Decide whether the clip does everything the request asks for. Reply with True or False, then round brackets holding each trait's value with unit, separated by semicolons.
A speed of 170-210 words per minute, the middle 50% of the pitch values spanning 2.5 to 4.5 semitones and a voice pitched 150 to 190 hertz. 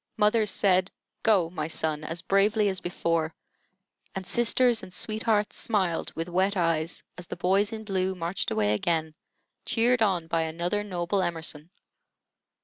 False (145 wpm; 3.8 semitones; 185 Hz)